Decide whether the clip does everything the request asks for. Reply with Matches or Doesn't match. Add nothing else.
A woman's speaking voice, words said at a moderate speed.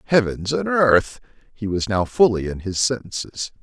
Doesn't match